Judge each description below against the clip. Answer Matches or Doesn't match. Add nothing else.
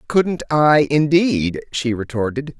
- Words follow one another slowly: Matches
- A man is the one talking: Matches